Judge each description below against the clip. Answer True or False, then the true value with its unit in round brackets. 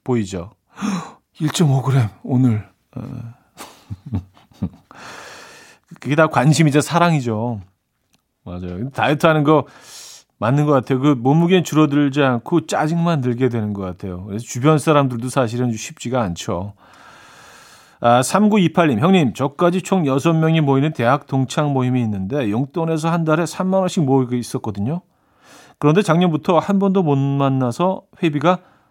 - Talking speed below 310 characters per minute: True (270 characters per minute)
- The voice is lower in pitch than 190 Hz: True (140 Hz)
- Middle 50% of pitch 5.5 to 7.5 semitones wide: False (5.1 semitones)